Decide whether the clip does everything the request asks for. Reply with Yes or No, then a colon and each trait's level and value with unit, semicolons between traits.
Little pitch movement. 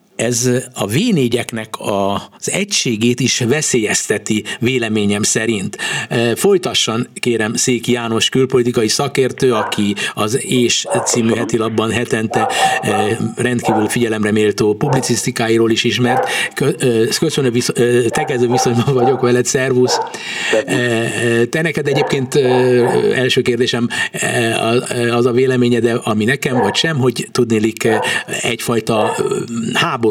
Yes: narrow, 1.9 semitones